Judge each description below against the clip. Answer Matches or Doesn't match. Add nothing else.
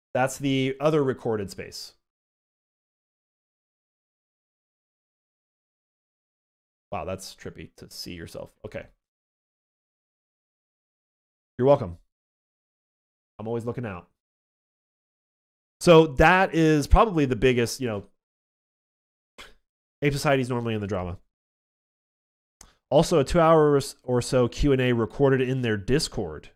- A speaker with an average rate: Doesn't match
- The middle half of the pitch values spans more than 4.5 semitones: Matches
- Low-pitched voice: Matches